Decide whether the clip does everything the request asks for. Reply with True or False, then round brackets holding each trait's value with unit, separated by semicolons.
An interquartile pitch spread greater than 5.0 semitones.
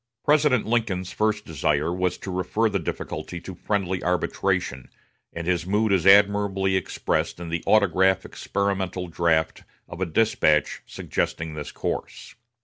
False (3.3 semitones)